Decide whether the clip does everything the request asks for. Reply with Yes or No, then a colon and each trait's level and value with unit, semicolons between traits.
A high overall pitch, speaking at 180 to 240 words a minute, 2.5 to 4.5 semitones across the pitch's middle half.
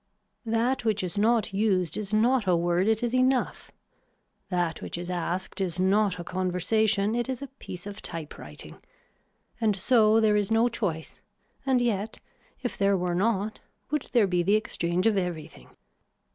No: high, 205 Hz; average, 165 wpm; average, 3.9 semitones